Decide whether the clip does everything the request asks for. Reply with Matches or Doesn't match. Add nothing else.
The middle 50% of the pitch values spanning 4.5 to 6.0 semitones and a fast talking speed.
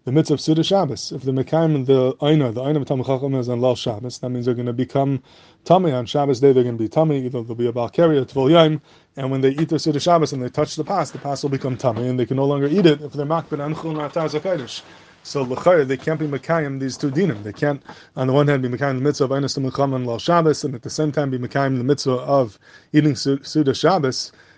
Doesn't match